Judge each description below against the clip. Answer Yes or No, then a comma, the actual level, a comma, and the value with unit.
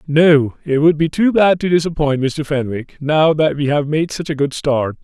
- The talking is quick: Yes, fast, 225 wpm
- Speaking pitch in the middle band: Yes, medium, 150 Hz